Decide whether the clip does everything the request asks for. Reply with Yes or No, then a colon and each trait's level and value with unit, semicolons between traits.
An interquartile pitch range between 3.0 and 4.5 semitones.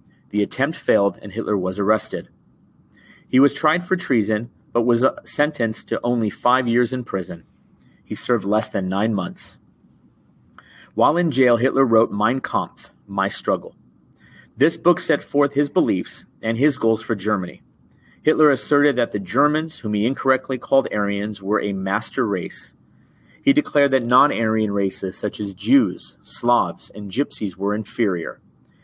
No: average, 5.1 semitones